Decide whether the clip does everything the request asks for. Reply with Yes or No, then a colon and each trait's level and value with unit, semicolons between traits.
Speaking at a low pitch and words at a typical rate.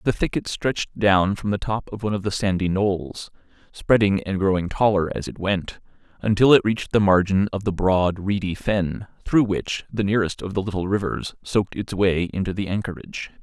Yes: low, 100 Hz; average, 195 wpm